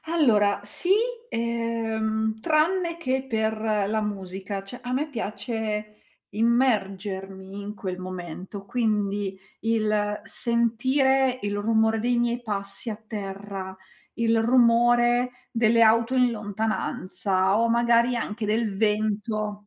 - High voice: Yes, high, 220 Hz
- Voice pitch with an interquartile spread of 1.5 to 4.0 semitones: Yes, narrow, 2.6 semitones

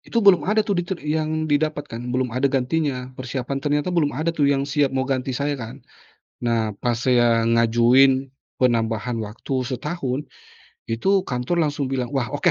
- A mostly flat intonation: No, average, 3.5 semitones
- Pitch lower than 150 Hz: Yes, low, 135 Hz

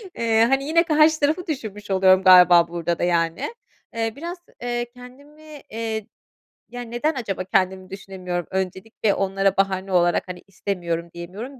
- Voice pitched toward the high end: Yes, high, 200 Hz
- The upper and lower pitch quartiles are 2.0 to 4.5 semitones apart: No, average, 5.2 semitones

